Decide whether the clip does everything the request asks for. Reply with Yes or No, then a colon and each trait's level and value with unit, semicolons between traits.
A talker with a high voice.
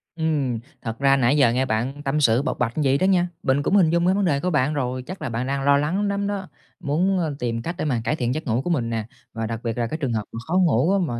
No: medium, 140 Hz